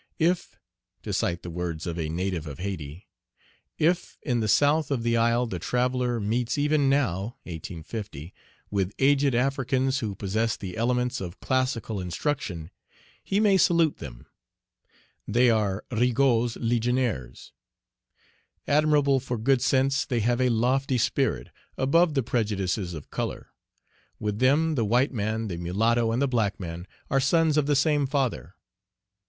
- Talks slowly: No, average, 150 wpm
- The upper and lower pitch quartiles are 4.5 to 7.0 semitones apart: Yes, wide, 5.5 semitones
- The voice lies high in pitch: No, low, 120 Hz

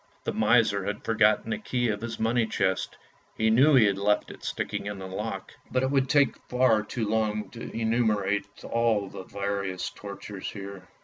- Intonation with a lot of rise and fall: No, average, 2.8 semitones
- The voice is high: No, low, 110 Hz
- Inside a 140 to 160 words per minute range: No, average, 185 wpm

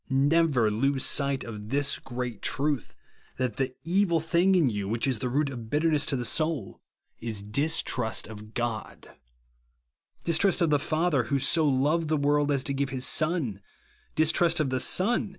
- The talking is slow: No, average, 180 wpm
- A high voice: No, medium, 140 Hz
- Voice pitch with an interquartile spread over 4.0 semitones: Yes, average, 4.5 semitones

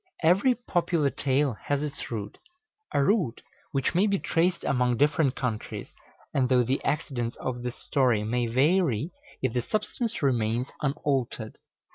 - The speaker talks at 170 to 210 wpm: No, average, 145 wpm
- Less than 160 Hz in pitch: Yes, low, 135 Hz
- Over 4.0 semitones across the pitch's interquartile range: Yes, average, 4.7 semitones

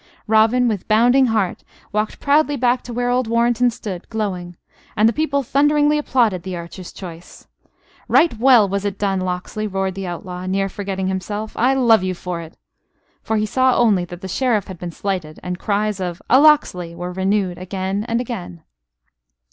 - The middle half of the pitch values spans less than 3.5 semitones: No, average, 4.7 semitones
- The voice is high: Yes, high, 205 Hz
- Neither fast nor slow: Yes, average, 180 wpm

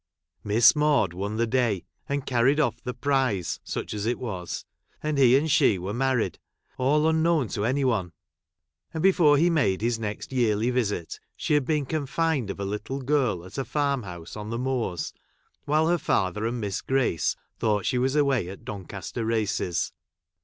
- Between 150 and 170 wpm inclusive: No, average, 180 wpm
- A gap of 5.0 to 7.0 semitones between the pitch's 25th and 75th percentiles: Yes, wide, 5.4 semitones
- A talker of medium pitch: No, low, 125 Hz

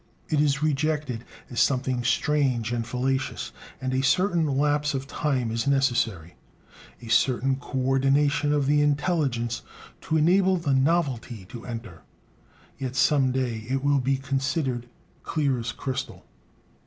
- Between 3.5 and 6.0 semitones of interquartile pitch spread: No, average, 3.0 semitones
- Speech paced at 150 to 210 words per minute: No, slow, 135 wpm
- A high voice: No, low, 135 Hz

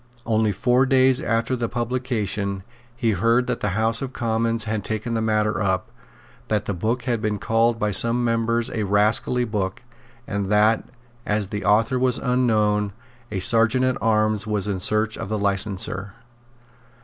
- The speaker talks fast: No, average, 165 wpm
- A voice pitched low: Yes, low, 110 Hz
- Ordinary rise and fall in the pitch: No, narrow, 2.2 semitones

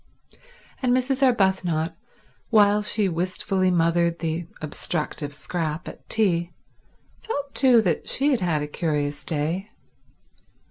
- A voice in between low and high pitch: Yes, medium, 175 Hz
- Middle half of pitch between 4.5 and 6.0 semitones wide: Yes, average, 4.9 semitones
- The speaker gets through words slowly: Yes, slow, 120 wpm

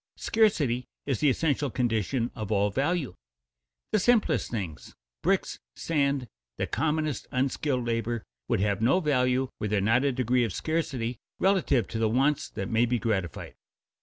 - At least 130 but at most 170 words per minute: Yes, average, 160 wpm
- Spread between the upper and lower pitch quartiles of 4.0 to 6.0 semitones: Yes, average, 4.4 semitones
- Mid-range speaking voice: No, low, 125 Hz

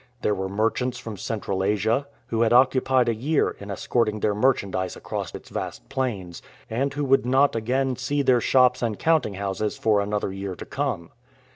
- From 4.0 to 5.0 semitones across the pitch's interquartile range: Yes, average, 4.4 semitones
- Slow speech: No, average, 180 wpm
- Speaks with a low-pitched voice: Yes, low, 115 Hz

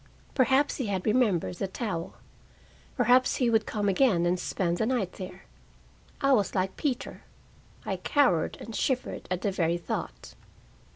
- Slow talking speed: No, average, 155 wpm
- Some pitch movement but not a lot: No, wide, 5.7 semitones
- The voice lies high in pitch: Yes, high, 205 Hz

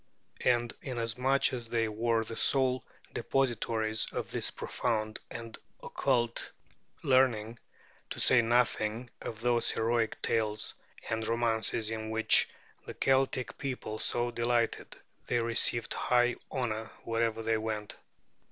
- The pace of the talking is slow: Yes, slow, 120 wpm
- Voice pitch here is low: Yes, low, 115 Hz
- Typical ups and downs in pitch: No, narrow, 1.6 semitones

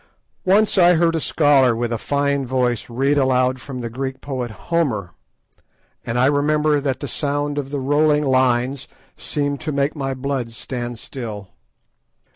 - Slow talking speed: No, average, 160 wpm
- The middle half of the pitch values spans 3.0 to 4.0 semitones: No, narrow, 2.6 semitones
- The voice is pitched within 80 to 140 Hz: Yes, low, 135 Hz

